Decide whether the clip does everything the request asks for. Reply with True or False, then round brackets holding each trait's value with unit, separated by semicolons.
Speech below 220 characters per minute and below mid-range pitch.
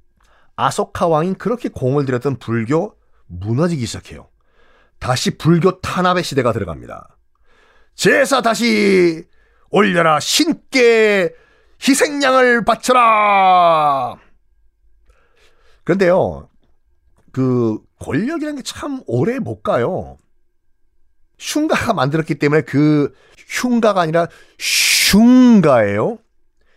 False (205 characters per minute; 180 Hz)